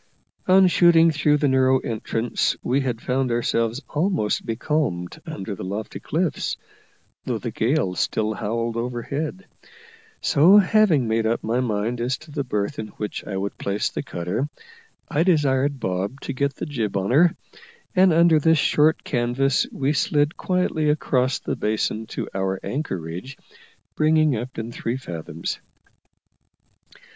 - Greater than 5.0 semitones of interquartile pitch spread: Yes, wide, 5.6 semitones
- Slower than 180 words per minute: Yes, average, 150 wpm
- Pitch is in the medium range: No, low, 130 Hz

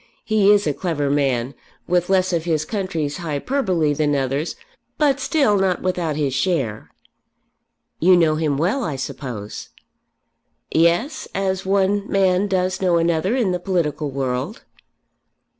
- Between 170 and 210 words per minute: No, average, 140 wpm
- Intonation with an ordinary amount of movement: Yes, average, 4.7 semitones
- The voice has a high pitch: No, medium, 175 Hz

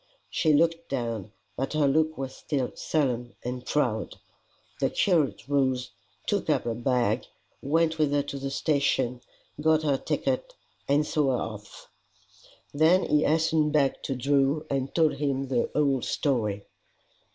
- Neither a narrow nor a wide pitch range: Yes, average, 3.4 semitones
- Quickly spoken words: No, average, 150 wpm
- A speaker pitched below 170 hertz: Yes, medium, 140 Hz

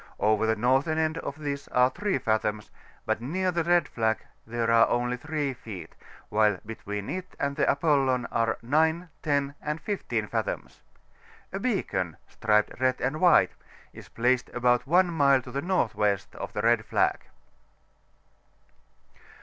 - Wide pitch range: Yes, wide, 5.8 semitones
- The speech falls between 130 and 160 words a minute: Yes, average, 150 wpm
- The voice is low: Yes, low, 130 Hz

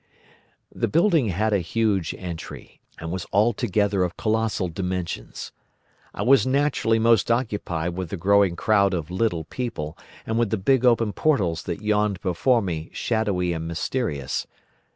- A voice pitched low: Yes, low, 100 Hz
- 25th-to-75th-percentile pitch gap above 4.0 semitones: Yes, average, 4.6 semitones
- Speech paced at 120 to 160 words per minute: Yes, average, 150 wpm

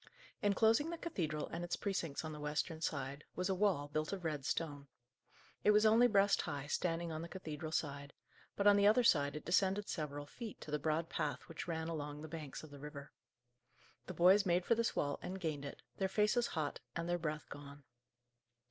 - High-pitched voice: No, medium, 165 Hz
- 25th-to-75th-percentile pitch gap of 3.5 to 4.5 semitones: No, average, 4.9 semitones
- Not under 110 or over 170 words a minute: No, fast, 205 wpm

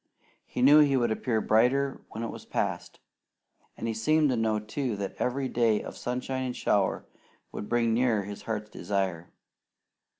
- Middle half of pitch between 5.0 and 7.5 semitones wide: No, average, 3.3 semitones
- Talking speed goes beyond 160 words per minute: Yes, average, 170 wpm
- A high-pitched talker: No, low, 115 Hz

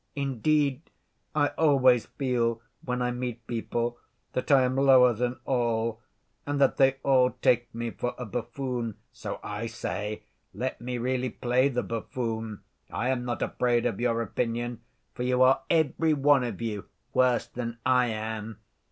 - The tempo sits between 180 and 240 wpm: No, average, 160 wpm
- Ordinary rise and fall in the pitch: No, narrow, 1.9 semitones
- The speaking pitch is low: Yes, low, 125 Hz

